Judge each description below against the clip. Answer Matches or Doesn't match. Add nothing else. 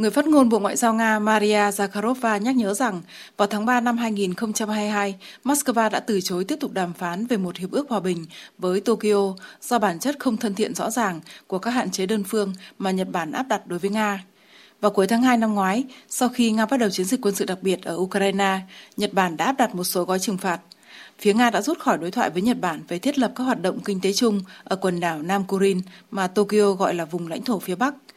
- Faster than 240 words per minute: Matches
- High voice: Matches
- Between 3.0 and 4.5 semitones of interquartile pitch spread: Matches